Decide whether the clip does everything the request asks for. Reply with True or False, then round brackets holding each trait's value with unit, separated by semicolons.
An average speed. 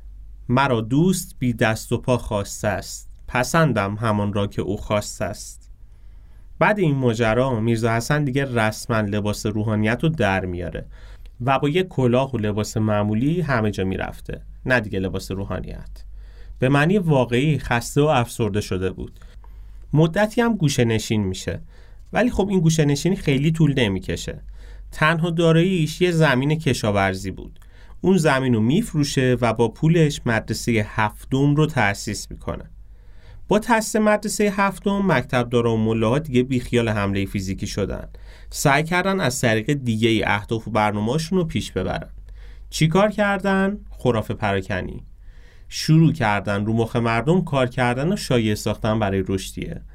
True (145 wpm)